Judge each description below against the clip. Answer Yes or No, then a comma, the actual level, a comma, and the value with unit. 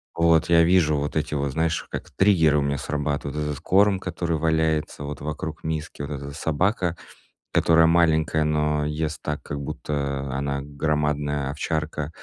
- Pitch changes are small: Yes, narrow, 1.9 semitones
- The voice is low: Yes, very low, 75 Hz